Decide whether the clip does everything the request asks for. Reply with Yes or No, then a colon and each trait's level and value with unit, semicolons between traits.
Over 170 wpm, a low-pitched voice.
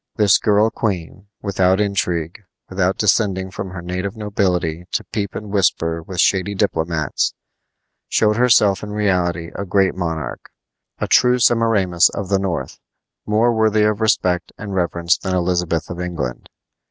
No: average, 145 wpm; very low, 95 Hz